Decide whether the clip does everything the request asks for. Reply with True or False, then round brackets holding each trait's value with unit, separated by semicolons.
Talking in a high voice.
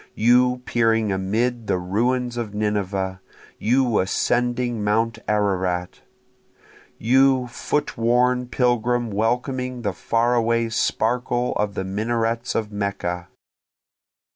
False (115 Hz)